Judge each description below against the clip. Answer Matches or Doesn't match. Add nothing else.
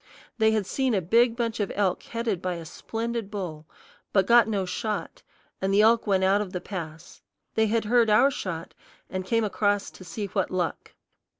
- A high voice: Matches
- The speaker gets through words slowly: Doesn't match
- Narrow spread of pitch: Doesn't match